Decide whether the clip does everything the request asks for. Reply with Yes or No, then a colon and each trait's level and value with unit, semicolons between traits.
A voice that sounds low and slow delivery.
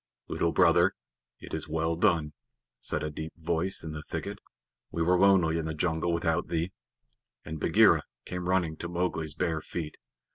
No: very low, 85 Hz; average, 170 wpm